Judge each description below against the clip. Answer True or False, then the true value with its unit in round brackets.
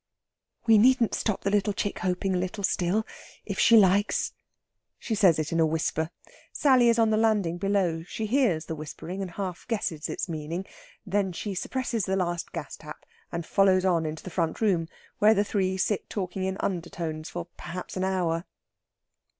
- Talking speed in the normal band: True (180 wpm)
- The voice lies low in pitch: False (190 Hz)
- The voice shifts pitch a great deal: False (3.4 semitones)